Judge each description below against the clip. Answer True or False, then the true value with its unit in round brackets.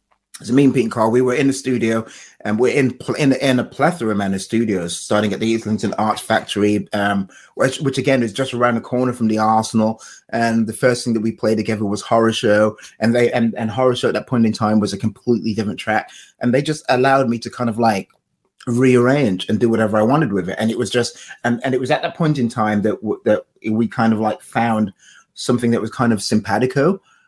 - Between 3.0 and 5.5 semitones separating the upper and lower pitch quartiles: False (2.6 semitones)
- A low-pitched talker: True (115 Hz)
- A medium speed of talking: False (240 wpm)